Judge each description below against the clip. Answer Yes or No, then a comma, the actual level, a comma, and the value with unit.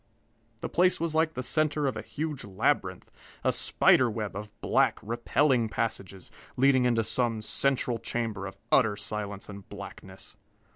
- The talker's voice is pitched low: Yes, low, 115 Hz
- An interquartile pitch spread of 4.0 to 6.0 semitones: Yes, average, 4.7 semitones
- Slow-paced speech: No, average, 150 wpm